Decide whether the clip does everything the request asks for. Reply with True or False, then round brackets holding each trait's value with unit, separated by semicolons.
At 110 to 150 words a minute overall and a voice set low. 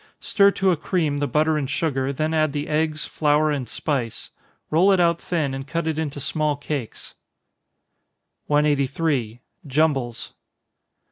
False (145 wpm; 150 Hz)